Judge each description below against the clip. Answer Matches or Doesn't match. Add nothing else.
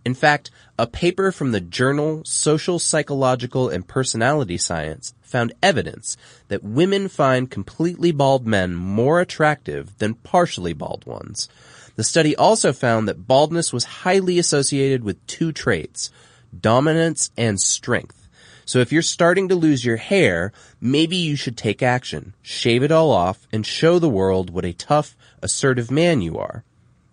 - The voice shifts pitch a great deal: Matches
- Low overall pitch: Matches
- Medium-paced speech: Matches